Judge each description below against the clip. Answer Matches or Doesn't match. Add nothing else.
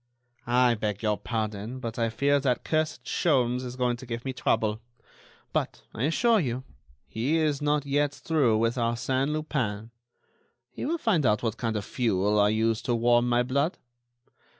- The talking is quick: Doesn't match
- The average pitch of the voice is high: Doesn't match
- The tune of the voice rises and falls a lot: Doesn't match